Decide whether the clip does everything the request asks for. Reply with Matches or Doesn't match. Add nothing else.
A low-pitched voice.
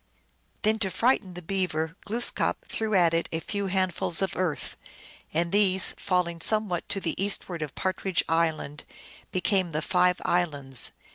Doesn't match